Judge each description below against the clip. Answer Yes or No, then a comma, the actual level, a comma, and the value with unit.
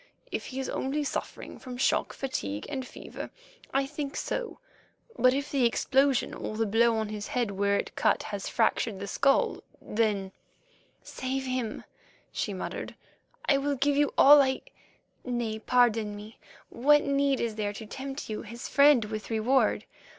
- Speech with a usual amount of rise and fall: Yes, average, 4.1 semitones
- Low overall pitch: No, high, 245 Hz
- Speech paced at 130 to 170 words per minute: Yes, average, 160 wpm